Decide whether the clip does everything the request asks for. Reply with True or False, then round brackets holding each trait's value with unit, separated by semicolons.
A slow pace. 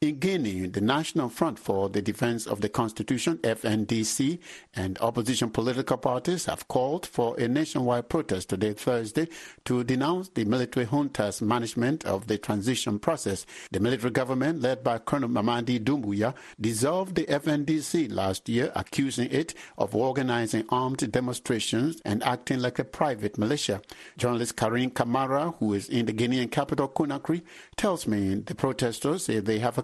False (155 wpm)